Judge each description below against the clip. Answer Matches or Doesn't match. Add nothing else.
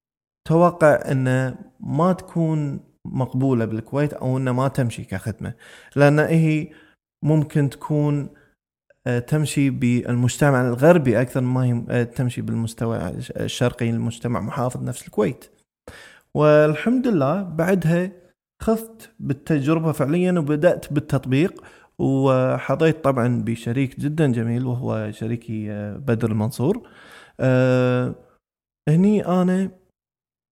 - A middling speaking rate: Doesn't match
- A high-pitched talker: Doesn't match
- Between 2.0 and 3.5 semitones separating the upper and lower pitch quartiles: Doesn't match